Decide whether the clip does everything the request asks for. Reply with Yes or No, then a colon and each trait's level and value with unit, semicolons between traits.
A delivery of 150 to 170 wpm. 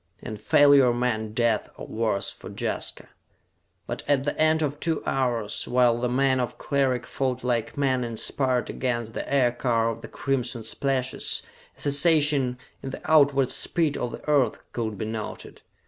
Yes: average, 165 wpm